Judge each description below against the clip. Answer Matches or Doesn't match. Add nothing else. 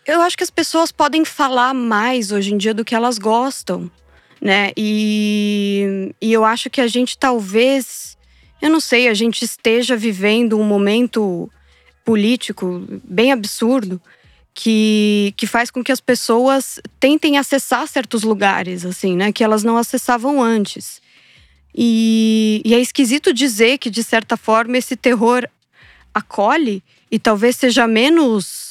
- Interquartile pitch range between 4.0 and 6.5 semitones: Doesn't match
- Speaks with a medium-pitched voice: Doesn't match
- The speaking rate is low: Doesn't match